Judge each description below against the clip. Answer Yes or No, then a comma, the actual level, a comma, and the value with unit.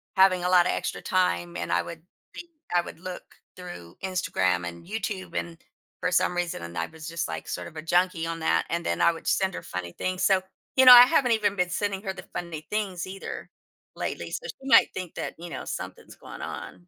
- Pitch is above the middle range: No, medium, 180 Hz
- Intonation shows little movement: No, average, 3.0 semitones